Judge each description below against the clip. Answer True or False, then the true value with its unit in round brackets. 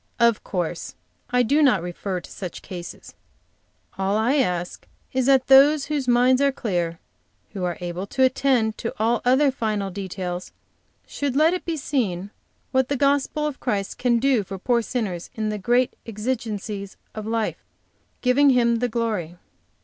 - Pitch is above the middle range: True (230 Hz)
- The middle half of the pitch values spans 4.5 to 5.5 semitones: True (5.0 semitones)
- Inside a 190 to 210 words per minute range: False (165 wpm)